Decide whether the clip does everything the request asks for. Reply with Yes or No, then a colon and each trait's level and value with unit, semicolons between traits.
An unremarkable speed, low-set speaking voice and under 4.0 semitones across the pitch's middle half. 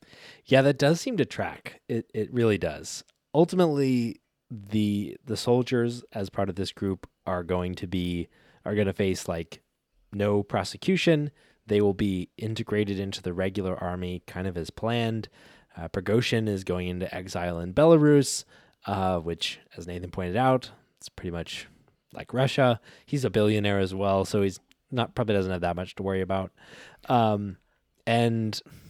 No: average, 165 wpm; low, 100 Hz; average, 4.3 semitones